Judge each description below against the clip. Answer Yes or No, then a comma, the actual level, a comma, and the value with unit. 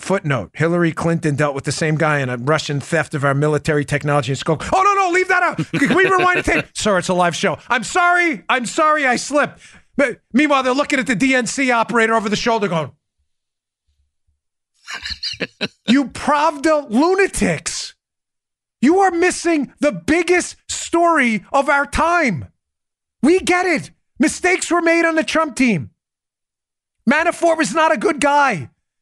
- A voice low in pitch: No, very high, 255 Hz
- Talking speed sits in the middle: Yes, average, 165 wpm